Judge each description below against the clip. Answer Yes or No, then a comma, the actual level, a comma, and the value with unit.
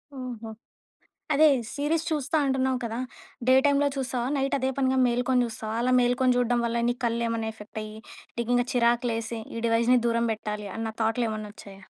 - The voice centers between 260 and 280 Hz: No, high, 240 Hz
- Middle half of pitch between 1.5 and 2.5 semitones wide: Yes, narrow, 2.2 semitones